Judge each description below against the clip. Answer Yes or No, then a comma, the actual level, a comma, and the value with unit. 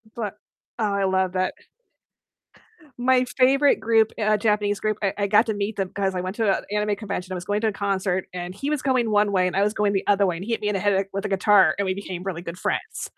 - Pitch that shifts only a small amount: Yes, narrow, 2.1 semitones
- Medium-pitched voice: No, high, 200 Hz